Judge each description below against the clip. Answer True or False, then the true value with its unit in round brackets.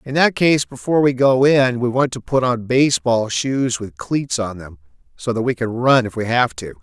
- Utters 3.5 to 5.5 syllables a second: True (4.9 syllables/s)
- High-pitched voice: False (125 Hz)